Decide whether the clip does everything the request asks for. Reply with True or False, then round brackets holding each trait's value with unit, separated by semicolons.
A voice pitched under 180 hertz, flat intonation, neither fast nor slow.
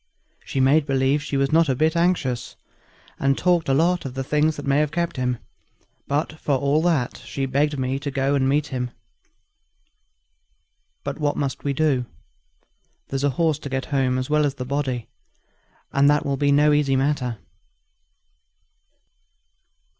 True (140 Hz; 2.1 semitones; 170 wpm)